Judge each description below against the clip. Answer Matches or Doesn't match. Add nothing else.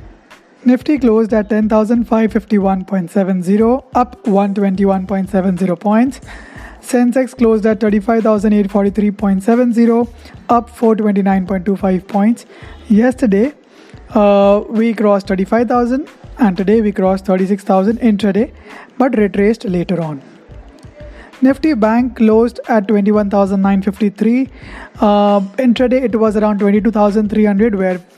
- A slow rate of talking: Matches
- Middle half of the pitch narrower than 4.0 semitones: Matches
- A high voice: Matches